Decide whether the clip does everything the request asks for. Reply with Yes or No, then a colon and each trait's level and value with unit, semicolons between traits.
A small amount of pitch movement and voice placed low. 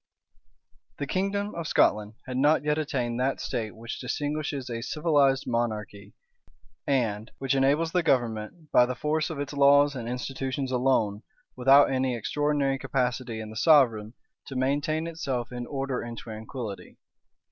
No: average, 3.5 semitones; low, 130 Hz